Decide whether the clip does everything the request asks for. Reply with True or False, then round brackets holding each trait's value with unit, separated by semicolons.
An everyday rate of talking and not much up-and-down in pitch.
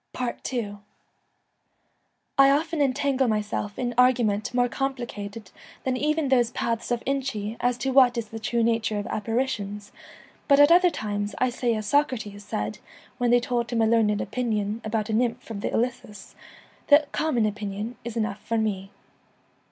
False (160 wpm; 3.4 semitones)